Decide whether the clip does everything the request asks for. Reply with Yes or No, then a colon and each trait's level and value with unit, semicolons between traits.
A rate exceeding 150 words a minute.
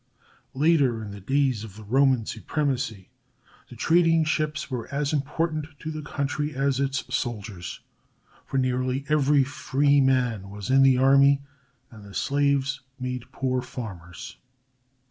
No: average, 140 wpm